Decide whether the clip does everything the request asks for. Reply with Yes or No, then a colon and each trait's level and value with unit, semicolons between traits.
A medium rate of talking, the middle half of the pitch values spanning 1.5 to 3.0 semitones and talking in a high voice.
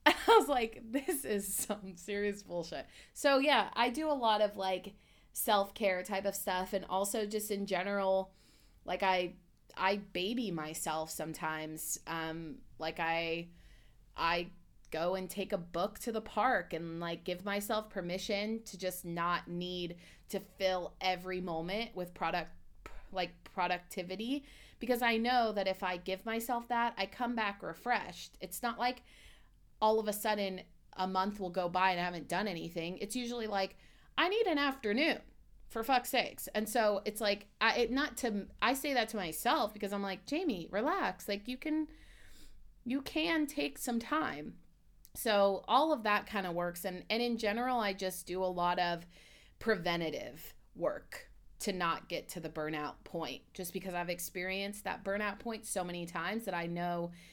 No: average, 175 wpm; average, 4.1 semitones; high, 195 Hz